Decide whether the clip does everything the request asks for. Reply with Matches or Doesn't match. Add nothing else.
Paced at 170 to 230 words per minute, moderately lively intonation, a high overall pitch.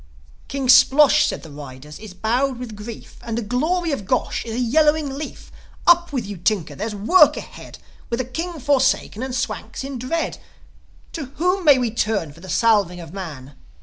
Doesn't match